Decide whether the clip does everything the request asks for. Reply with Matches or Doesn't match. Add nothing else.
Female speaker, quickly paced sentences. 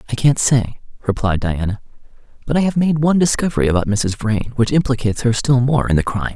Doesn't match